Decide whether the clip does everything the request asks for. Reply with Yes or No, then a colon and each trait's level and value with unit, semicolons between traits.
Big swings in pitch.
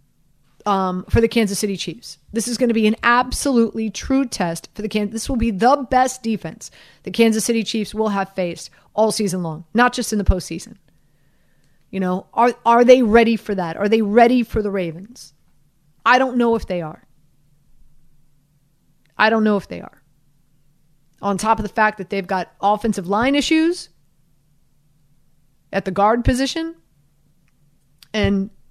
Yes: wide, 6.6 semitones